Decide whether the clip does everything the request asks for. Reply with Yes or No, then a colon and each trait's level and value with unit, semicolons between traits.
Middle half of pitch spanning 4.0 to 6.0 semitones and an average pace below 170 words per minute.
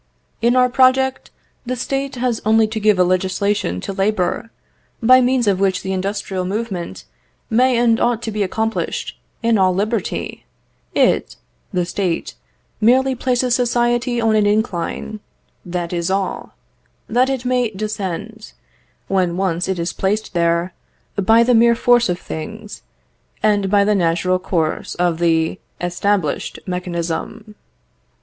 Yes: average, 4.5 semitones; average, 140 wpm